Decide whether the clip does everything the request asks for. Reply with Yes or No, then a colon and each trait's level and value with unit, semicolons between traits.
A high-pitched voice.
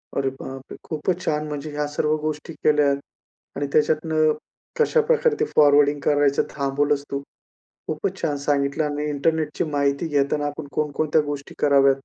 No: medium, 150 Hz